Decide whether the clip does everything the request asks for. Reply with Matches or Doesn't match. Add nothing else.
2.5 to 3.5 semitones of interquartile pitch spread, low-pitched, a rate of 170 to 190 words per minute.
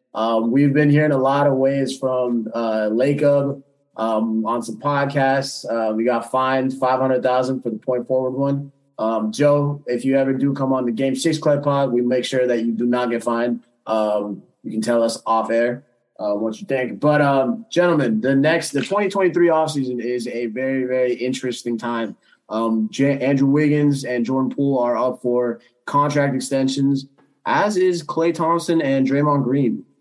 Matches